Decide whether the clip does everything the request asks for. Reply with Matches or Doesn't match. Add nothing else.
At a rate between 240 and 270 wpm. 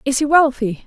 Doesn't match